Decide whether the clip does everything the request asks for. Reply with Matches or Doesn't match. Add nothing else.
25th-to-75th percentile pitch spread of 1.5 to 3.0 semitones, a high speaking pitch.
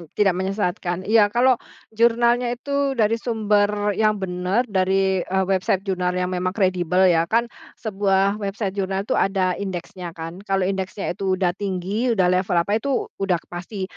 Matches